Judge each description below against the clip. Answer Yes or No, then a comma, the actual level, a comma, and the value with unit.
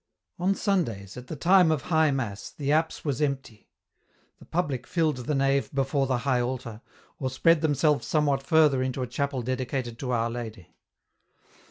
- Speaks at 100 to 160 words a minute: No, average, 170 wpm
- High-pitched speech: No, low, 135 Hz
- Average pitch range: Yes, average, 3.7 semitones